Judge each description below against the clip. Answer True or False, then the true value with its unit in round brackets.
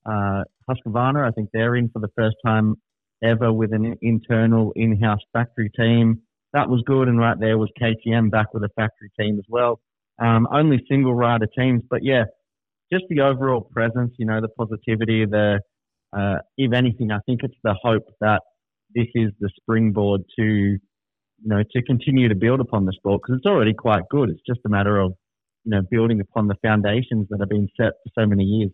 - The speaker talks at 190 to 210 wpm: True (200 wpm)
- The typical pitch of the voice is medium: False (110 Hz)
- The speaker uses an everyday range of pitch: False (2.3 semitones)